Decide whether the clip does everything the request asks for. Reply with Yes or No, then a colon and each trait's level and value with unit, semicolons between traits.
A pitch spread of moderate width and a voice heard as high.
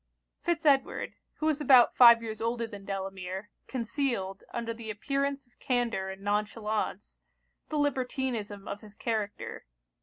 Yes: average, 4.4 semitones; high, 230 Hz